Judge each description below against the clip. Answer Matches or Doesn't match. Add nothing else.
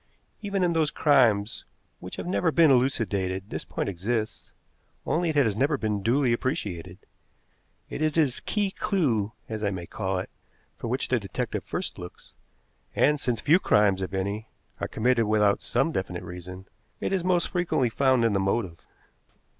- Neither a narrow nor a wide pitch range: Doesn't match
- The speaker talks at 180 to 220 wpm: Doesn't match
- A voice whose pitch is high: Doesn't match